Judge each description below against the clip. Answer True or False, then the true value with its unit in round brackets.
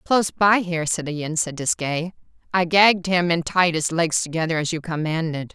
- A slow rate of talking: False (185 wpm)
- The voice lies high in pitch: False (170 Hz)